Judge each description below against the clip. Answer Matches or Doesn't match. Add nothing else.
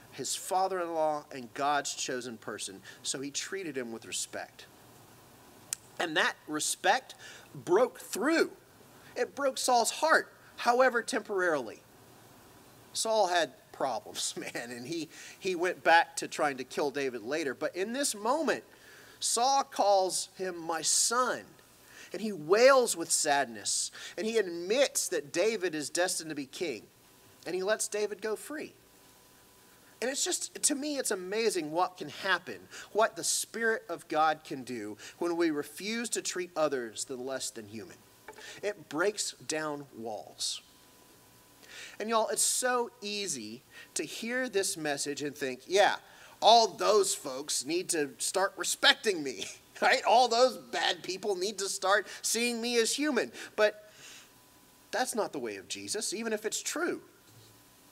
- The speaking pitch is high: Matches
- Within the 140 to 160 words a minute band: Matches